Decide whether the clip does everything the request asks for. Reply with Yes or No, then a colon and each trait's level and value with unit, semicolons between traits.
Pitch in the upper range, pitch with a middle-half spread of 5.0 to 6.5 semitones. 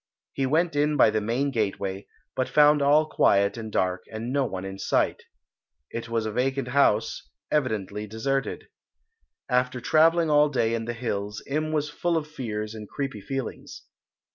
No: low, 125 Hz; average, 5.3 semitones